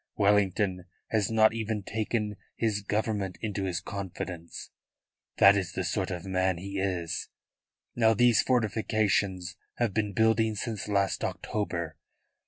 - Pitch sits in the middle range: No, low, 100 Hz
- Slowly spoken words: Yes, slow, 130 wpm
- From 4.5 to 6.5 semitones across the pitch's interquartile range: No, narrow, 2.6 semitones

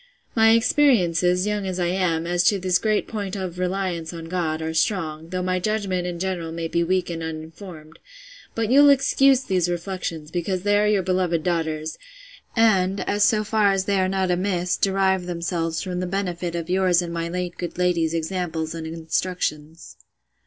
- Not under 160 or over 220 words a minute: Yes, average, 180 wpm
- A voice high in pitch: No, medium, 180 Hz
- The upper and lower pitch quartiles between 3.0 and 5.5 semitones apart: No, narrow, 2.6 semitones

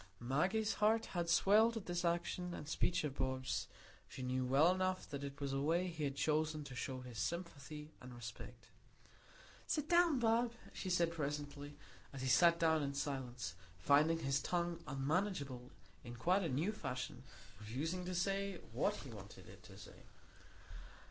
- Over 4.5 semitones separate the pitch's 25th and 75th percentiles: Yes, average, 5.0 semitones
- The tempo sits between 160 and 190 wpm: Yes, average, 170 wpm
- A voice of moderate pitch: Yes, medium, 155 Hz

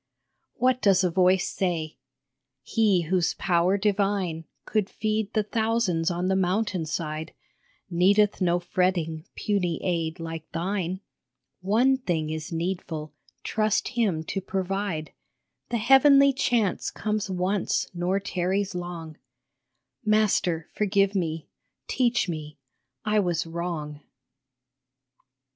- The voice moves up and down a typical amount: Yes, average, 4.0 semitones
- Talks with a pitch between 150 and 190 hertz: Yes, medium, 185 Hz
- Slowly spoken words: Yes, slow, 115 wpm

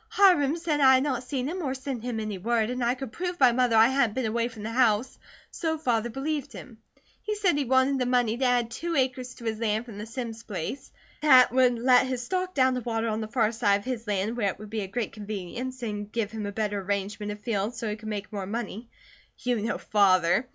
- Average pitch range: Yes, average, 3.4 semitones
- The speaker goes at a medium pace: No, fast, 250 wpm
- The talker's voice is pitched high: Yes, high, 235 Hz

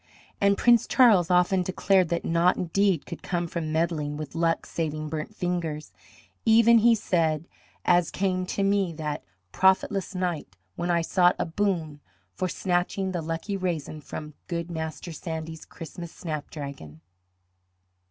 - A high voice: No, medium, 170 Hz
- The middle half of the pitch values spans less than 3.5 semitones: Yes, average, 2.9 semitones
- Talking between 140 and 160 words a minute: Yes, average, 145 wpm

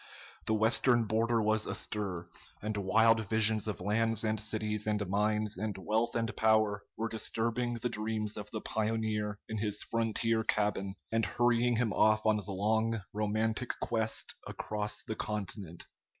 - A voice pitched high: No, low, 110 Hz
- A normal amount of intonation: No, narrow, 1.2 semitones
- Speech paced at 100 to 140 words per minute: No, average, 150 wpm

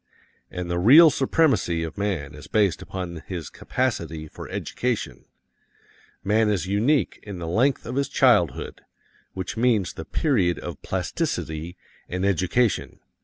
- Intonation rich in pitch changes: Yes, wide, 5.9 semitones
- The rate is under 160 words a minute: Yes, slow, 135 wpm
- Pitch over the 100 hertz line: No, very low, 95 Hz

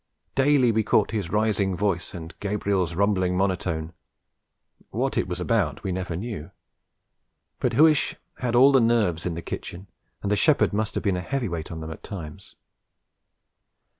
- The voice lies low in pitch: Yes, low, 100 Hz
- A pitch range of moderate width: Yes, average, 4.2 semitones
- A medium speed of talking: Yes, average, 165 wpm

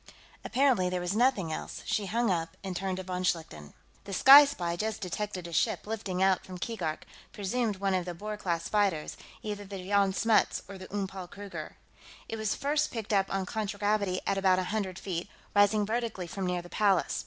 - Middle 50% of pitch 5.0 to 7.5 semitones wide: No, average, 2.7 semitones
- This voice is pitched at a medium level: No, high, 195 Hz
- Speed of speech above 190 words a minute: Yes, average, 200 wpm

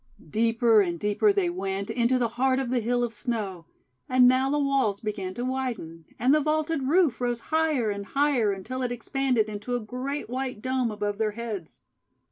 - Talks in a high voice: Yes, high, 245 Hz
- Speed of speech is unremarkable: Yes, average, 190 wpm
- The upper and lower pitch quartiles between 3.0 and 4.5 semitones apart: Yes, average, 3.9 semitones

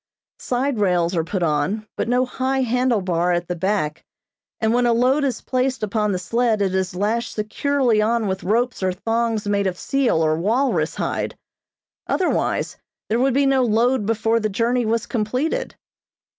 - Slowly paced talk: No, average, 175 wpm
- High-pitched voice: Yes, high, 225 Hz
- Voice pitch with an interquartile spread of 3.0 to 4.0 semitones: No, average, 4.4 semitones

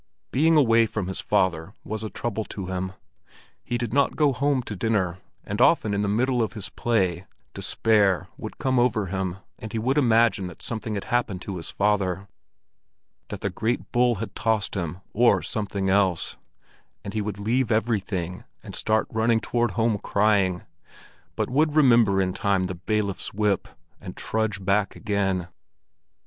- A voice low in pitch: Yes, low, 105 Hz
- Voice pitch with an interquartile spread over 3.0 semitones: Yes, average, 3.5 semitones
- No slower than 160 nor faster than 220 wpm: Yes, average, 165 wpm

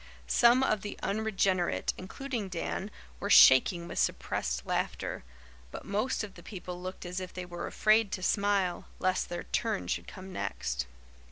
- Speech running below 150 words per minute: No, average, 160 wpm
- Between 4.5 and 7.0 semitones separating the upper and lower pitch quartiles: No, average, 2.9 semitones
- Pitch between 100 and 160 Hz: No, high, 190 Hz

